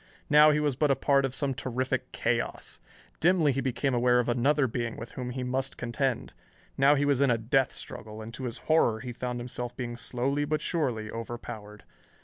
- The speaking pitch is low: Yes, low, 125 Hz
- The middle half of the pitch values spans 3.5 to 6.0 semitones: No, average, 2.7 semitones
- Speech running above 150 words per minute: Yes, average, 200 wpm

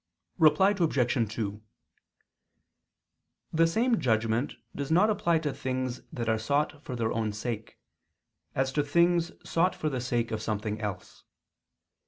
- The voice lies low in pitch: Yes, low, 130 Hz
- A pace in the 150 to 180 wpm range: No, average, 140 wpm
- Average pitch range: No, wide, 6.5 semitones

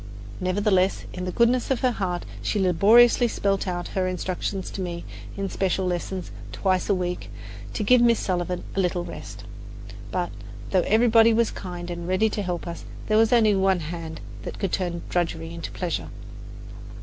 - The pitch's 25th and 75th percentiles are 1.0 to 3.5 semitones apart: Yes, average, 3.2 semitones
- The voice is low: No, medium, 185 Hz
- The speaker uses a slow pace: No, average, 175 wpm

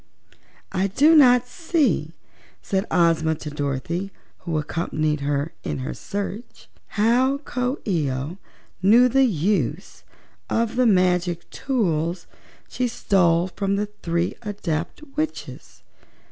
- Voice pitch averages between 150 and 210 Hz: Yes, medium, 185 Hz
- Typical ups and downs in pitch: No, wide, 6.7 semitones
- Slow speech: Yes, slow, 120 wpm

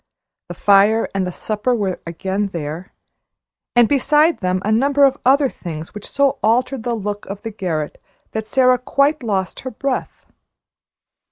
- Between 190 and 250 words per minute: No, average, 160 wpm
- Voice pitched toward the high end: Yes, high, 220 Hz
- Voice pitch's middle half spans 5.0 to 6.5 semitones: Yes, average, 5.3 semitones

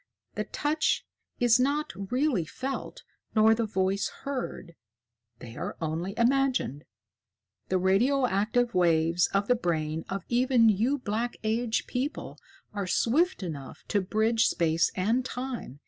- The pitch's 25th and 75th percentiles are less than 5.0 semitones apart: No, wide, 5.4 semitones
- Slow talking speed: Yes, slow, 130 wpm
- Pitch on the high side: Yes, high, 220 Hz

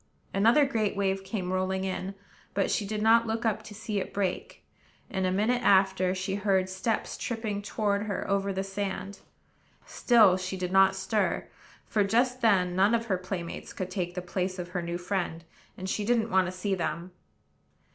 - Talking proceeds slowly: No, average, 185 wpm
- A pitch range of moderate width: No, narrow, 2.3 semitones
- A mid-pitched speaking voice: No, high, 195 Hz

